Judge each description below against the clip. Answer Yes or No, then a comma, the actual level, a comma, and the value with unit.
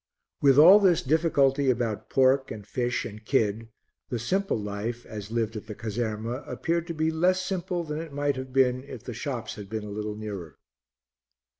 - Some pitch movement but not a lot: No, wide, 5.7 semitones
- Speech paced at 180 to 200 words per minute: Yes, average, 185 wpm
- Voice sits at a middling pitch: No, low, 125 Hz